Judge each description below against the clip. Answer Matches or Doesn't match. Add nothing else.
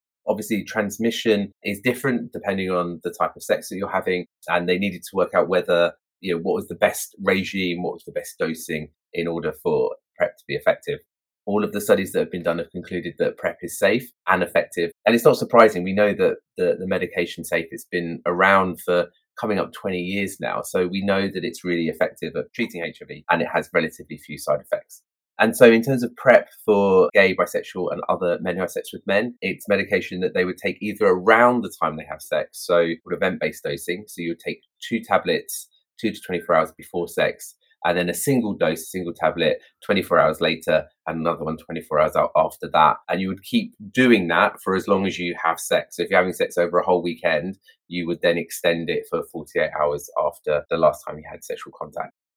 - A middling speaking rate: Doesn't match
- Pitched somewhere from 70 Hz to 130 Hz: Matches